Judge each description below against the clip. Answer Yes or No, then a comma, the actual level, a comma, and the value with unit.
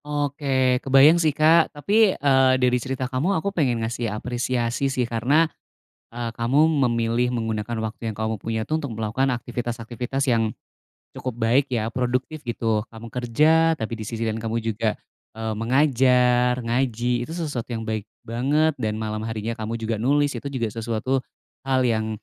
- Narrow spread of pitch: No, average, 3.1 semitones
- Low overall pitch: Yes, low, 120 Hz